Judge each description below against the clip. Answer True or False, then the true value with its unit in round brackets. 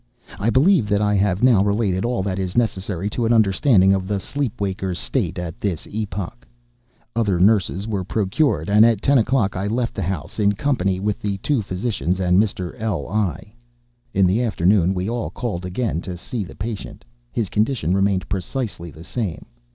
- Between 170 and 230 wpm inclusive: True (180 wpm)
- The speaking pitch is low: True (100 Hz)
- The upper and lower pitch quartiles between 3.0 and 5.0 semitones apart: True (3.3 semitones)